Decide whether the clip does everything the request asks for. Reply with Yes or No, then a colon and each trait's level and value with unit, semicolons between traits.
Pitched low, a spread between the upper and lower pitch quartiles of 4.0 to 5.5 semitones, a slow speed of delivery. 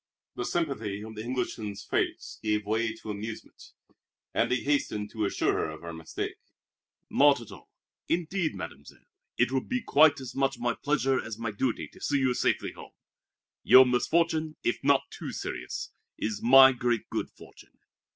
No: low, 125 Hz; average, 4.3 semitones; average, 170 wpm